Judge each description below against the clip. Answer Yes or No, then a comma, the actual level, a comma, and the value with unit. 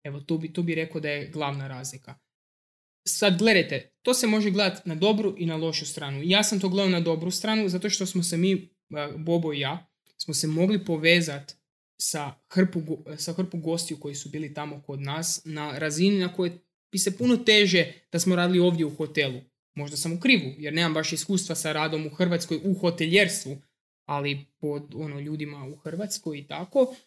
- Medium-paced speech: No, fast, 195 wpm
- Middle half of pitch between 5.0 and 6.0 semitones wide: No, average, 3.9 semitones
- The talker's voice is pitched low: No, medium, 165 Hz